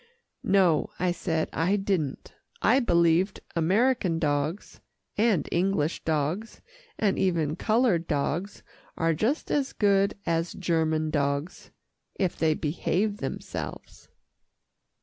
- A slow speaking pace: Yes, slow, 110 wpm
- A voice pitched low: No, medium, 175 Hz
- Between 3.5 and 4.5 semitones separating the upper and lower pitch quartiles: Yes, average, 4.0 semitones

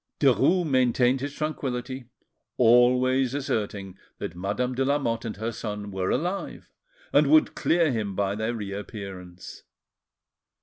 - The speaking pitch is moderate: No, low, 120 Hz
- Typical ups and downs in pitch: Yes, average, 4.6 semitones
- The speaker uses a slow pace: Yes, slow, 125 wpm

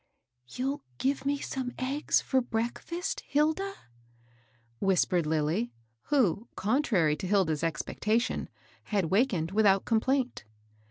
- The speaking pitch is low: No, high, 220 Hz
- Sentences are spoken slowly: Yes, slow, 115 wpm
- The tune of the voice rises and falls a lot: Yes, wide, 7.9 semitones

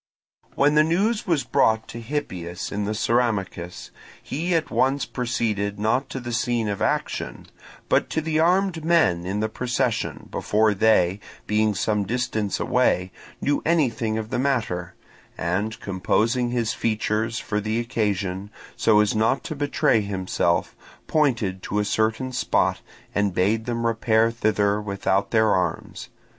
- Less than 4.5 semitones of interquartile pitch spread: Yes, average, 3.6 semitones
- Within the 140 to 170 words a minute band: Yes, average, 150 wpm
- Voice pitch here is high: No, low, 110 Hz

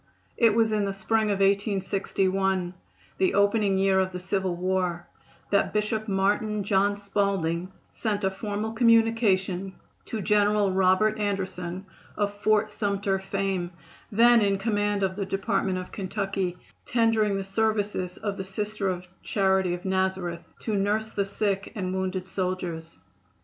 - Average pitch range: No, narrow, 1.8 semitones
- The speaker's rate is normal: Yes, average, 145 wpm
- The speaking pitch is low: No, high, 195 Hz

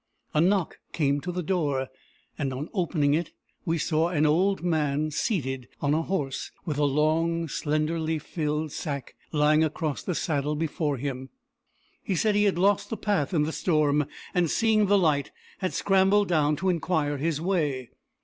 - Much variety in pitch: No, average, 3.5 semitones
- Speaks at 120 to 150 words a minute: No, average, 170 wpm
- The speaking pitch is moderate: Yes, medium, 155 Hz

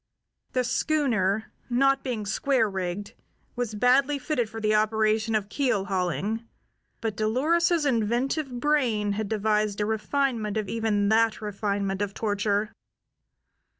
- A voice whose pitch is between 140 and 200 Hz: No, high, 220 Hz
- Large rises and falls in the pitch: No, average, 3.4 semitones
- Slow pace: Yes, slow, 125 wpm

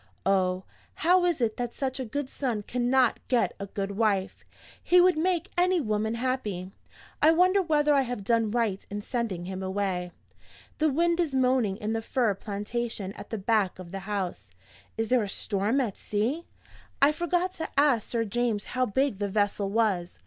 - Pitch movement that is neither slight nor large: No, wide, 5.7 semitones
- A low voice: No, high, 230 Hz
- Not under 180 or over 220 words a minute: Yes, average, 185 wpm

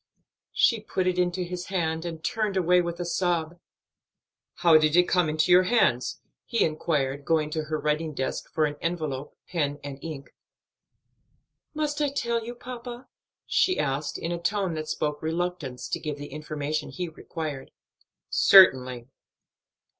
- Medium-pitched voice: Yes, medium, 165 Hz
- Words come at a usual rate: Yes, average, 155 wpm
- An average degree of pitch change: Yes, average, 3.3 semitones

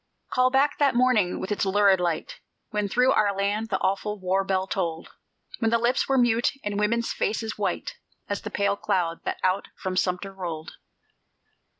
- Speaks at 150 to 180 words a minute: Yes, average, 175 wpm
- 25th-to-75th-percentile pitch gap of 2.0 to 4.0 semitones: Yes, average, 3.5 semitones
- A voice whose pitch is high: Yes, high, 205 Hz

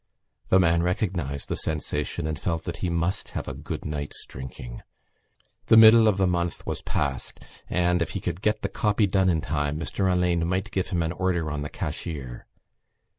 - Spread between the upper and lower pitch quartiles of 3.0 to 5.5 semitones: Yes, average, 3.7 semitones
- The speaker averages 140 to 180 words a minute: No, average, 190 wpm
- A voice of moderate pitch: No, very low, 85 Hz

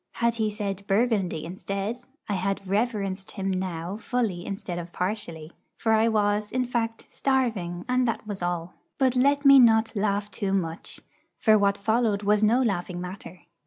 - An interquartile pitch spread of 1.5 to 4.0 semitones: Yes, average, 3.4 semitones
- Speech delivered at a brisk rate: No, average, 165 wpm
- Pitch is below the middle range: No, high, 205 Hz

